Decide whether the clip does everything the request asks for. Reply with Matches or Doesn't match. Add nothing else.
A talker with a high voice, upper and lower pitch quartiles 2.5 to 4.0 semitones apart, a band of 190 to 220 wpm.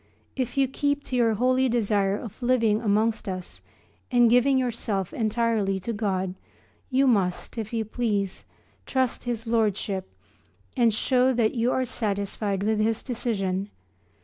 Doesn't match